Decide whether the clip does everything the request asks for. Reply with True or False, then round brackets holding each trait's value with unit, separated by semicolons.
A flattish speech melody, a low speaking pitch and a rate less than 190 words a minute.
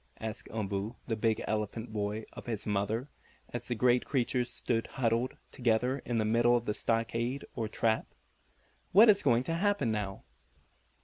True (2.3 semitones; 115 Hz; 165 wpm)